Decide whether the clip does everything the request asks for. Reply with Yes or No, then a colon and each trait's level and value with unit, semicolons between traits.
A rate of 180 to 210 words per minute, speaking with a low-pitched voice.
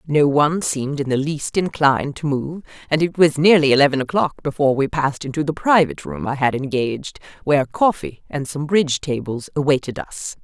No: average, 190 wpm; medium, 145 Hz